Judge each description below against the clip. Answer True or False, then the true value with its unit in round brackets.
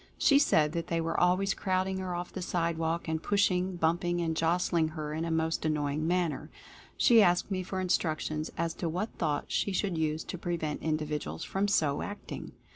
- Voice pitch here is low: False (170 Hz)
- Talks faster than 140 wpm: True (195 wpm)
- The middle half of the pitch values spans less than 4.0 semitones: True (2.7 semitones)